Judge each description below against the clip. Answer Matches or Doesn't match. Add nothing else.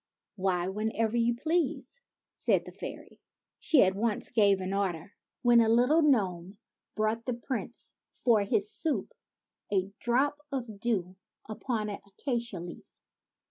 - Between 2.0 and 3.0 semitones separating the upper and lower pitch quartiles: Doesn't match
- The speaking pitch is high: Matches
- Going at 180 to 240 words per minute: Doesn't match